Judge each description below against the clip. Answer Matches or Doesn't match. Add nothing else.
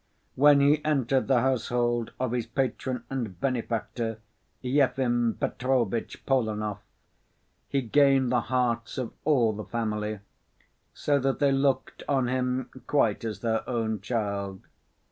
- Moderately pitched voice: Doesn't match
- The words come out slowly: Matches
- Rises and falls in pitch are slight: Doesn't match